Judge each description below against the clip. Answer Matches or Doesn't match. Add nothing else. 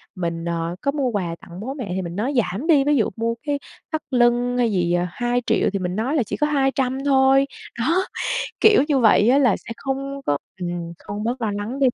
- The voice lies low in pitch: Doesn't match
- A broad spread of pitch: Matches